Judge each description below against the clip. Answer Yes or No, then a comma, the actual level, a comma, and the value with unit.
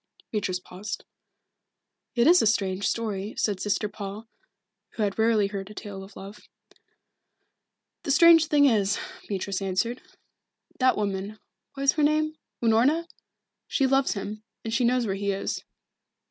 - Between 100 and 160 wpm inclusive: Yes, average, 150 wpm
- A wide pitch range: No, average, 4.6 semitones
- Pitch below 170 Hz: No, high, 215 Hz